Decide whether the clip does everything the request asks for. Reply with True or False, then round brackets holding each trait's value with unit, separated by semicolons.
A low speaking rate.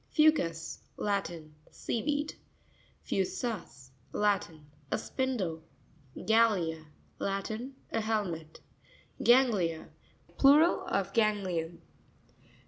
True (60 wpm)